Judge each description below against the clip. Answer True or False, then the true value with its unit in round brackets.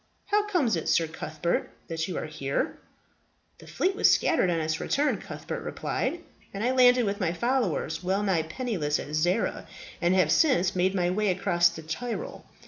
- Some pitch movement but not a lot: False (7.0 semitones)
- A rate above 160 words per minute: True (180 wpm)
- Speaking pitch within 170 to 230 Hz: True (185 Hz)